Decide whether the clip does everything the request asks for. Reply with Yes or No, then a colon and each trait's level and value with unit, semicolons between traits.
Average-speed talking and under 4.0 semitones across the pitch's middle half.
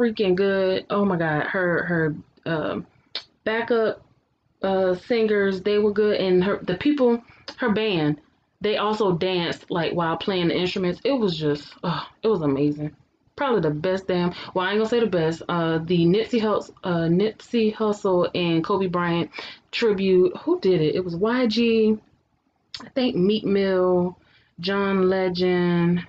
Yes: average, 160 wpm; average, 3.5 semitones